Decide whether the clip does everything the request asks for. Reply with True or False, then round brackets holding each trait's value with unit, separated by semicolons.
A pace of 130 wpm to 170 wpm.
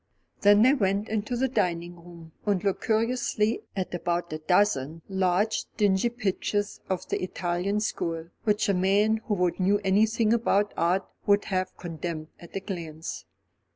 True (155 wpm)